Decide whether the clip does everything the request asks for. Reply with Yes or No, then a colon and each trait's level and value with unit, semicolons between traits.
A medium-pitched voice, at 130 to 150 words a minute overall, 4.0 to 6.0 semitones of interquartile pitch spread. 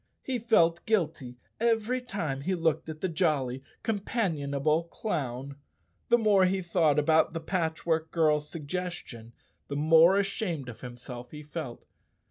Yes: medium, 160 Hz; average, 140 wpm; average, 4.8 semitones